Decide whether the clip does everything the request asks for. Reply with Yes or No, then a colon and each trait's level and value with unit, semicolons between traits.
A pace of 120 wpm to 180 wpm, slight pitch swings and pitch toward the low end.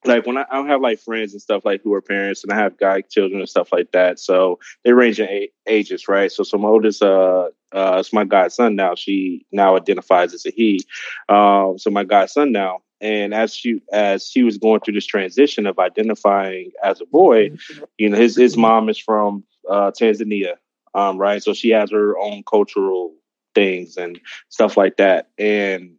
No: fast, 205 wpm; narrow, 2.3 semitones; low, 100 Hz